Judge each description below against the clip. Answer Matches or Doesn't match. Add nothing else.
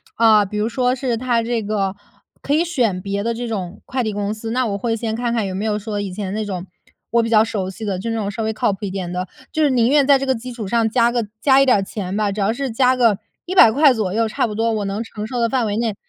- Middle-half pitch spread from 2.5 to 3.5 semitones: Matches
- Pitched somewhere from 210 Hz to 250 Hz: Matches